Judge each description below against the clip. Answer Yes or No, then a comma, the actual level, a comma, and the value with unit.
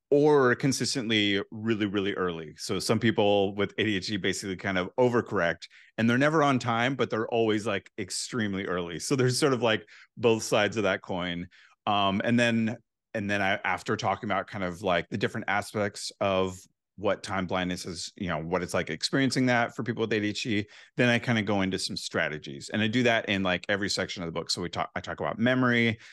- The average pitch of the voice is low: Yes, low, 105 Hz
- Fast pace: Yes, fast, 210 wpm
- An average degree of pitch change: Yes, average, 3.8 semitones